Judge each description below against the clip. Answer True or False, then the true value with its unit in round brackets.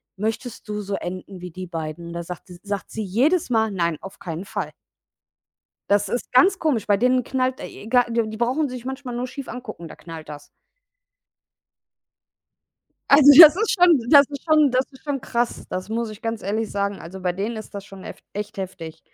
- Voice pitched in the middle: False (220 Hz)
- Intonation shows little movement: False (5.1 semitones)